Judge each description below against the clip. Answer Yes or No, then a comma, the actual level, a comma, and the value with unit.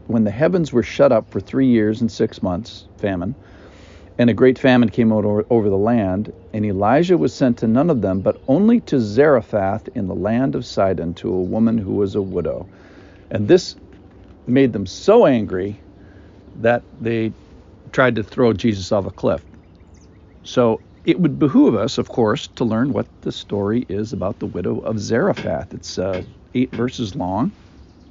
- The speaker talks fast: No, average, 180 wpm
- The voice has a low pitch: Yes, low, 105 Hz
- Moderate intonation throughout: Yes, average, 3.8 semitones